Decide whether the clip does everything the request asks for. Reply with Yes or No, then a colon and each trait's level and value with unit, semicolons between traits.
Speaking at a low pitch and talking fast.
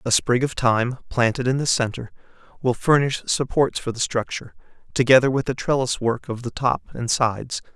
No: low, 125 Hz; average, 185 wpm